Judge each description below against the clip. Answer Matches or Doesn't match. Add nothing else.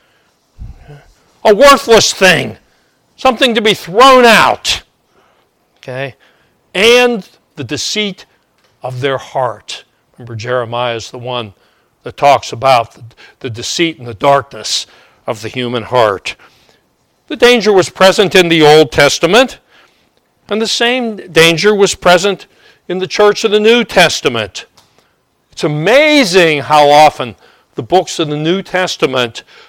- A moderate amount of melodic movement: Doesn't match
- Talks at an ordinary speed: Doesn't match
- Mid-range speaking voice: Matches